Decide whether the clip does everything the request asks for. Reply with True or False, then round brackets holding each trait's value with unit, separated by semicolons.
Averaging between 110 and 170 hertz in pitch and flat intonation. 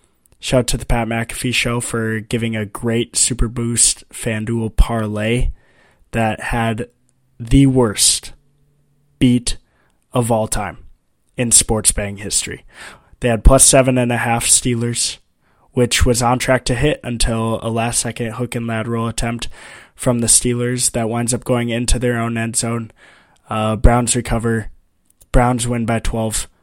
True (115 Hz; 1.7 semitones)